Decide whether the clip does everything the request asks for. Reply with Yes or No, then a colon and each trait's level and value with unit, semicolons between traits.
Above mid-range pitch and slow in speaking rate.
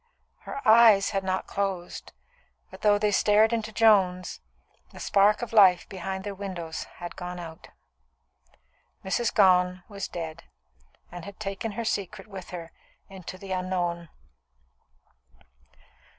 Yes: high, 195 Hz; slow, 130 wpm